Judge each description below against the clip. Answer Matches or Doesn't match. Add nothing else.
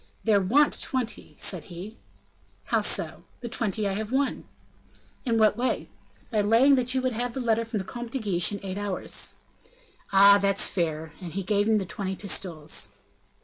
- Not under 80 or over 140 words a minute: Doesn't match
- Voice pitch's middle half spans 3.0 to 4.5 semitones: Matches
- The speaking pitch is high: Matches